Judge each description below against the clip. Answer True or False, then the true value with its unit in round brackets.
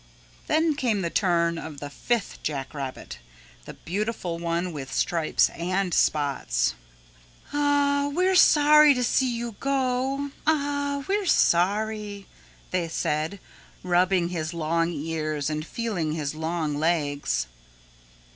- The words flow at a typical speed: False (125 wpm)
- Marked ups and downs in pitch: True (8.6 semitones)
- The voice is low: False (180 Hz)